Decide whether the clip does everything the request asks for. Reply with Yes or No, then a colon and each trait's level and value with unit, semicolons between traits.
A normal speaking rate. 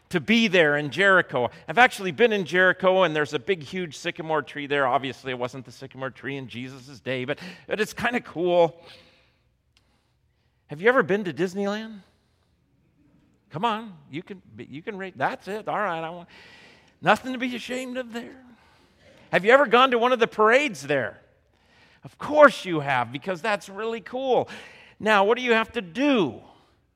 Yes: average, 185 wpm